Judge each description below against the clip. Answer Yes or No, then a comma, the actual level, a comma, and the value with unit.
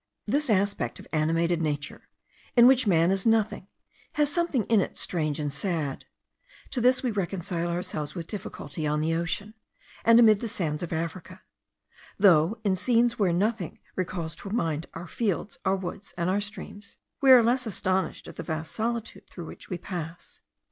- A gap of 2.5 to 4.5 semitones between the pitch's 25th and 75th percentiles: No, average, 5.0 semitones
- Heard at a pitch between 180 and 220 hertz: Yes, medium, 185 Hz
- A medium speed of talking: Yes, average, 175 wpm